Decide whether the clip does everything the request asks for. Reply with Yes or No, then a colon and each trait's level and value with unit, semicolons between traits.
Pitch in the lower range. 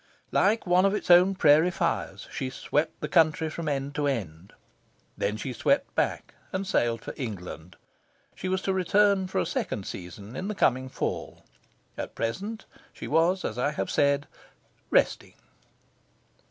No: medium, 150 Hz